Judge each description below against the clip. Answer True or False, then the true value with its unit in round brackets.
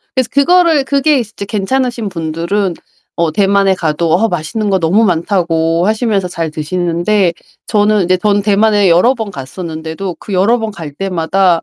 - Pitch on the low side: False (195 Hz)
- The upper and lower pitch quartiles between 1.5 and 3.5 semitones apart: False (4.2 semitones)